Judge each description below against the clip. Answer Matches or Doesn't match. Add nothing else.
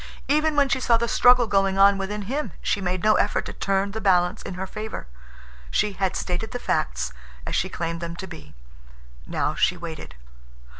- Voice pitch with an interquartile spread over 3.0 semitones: Matches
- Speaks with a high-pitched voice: Matches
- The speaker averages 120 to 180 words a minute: Doesn't match